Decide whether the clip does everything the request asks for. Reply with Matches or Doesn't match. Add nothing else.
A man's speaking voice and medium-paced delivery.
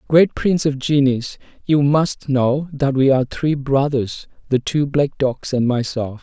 Matches